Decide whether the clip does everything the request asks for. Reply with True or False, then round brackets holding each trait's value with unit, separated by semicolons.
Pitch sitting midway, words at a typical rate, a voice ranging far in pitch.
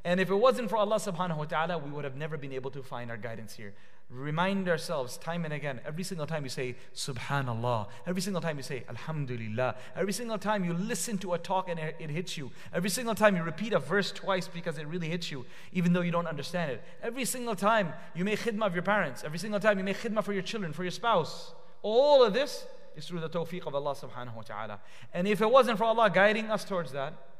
False (170 Hz; 245 wpm; 6.4 semitones)